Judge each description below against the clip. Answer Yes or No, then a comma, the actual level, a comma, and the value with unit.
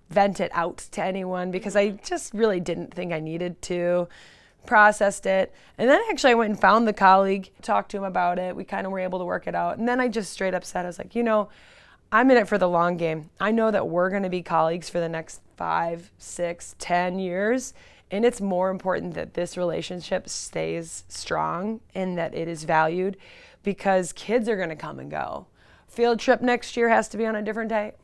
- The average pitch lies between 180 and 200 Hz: Yes, high, 190 Hz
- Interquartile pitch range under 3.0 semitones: No, average, 3.4 semitones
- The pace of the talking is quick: Yes, fast, 225 wpm